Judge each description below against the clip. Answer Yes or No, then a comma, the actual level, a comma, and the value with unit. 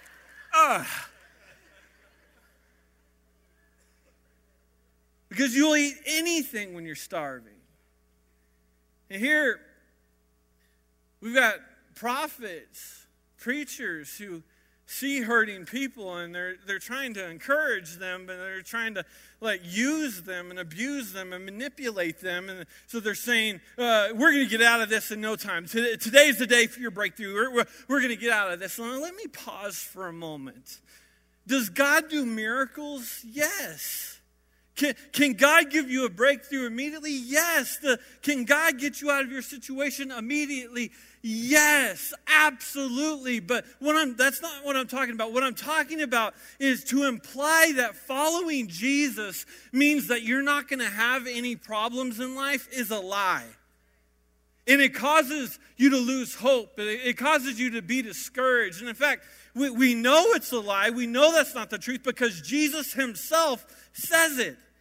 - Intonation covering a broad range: Yes, wide, 6.6 semitones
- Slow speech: No, average, 155 wpm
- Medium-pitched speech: No, high, 245 Hz